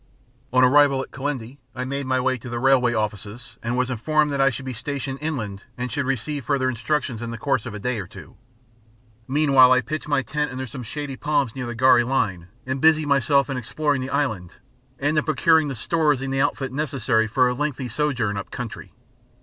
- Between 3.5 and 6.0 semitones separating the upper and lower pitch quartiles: No, average, 3.1 semitones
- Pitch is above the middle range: No, low, 130 Hz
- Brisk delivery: Yes, fast, 215 wpm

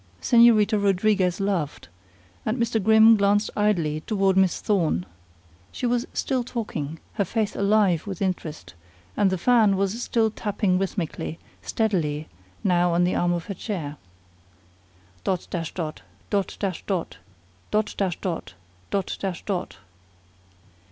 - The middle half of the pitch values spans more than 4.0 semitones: No, average, 3.5 semitones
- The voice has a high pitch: Yes, high, 195 Hz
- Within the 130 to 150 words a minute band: Yes, slow, 135 wpm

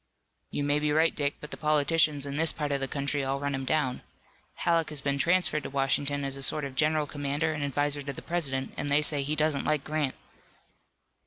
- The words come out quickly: Yes, fast, 225 wpm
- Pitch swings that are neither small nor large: No, narrow, 1.6 semitones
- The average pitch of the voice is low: No, medium, 145 Hz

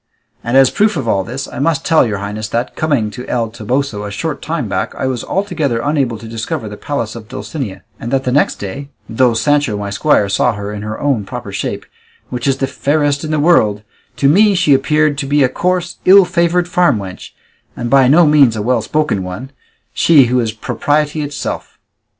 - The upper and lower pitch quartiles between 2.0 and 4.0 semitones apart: No, wide, 5.5 semitones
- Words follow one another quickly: Yes, fast, 215 wpm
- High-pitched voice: No, low, 130 Hz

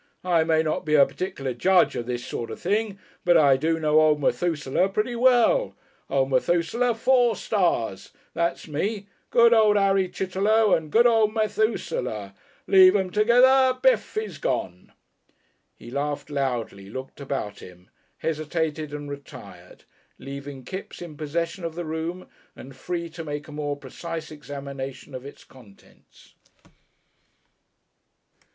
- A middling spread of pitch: No, wide, 6.2 semitones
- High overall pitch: No, medium, 160 Hz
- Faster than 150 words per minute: No, average, 140 wpm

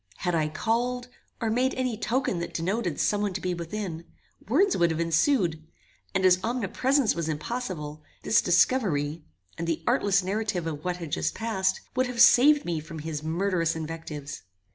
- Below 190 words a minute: Yes, average, 170 wpm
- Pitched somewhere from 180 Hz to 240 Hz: Yes, medium, 185 Hz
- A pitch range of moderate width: No, wide, 6.1 semitones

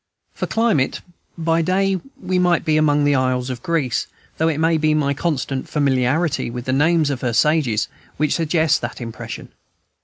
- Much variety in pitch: No, average, 4.0 semitones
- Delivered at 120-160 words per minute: No, average, 175 wpm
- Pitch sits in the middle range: Yes, medium, 150 Hz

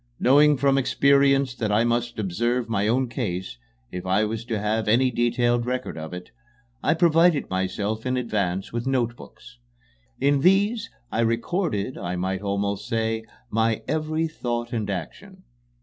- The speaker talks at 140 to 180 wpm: Yes, average, 150 wpm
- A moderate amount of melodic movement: Yes, average, 4.5 semitones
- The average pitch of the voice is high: No, low, 120 Hz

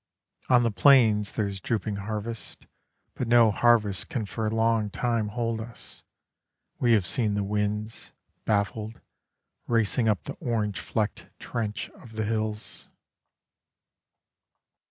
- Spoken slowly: Yes, slow, 125 wpm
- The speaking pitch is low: Yes, low, 110 Hz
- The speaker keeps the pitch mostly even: Yes, narrow, 1.8 semitones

